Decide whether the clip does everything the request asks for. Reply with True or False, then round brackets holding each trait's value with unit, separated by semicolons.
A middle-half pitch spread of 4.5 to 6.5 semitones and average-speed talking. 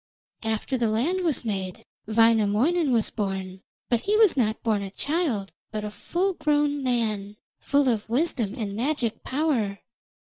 True (5.6 semitones; 150 wpm)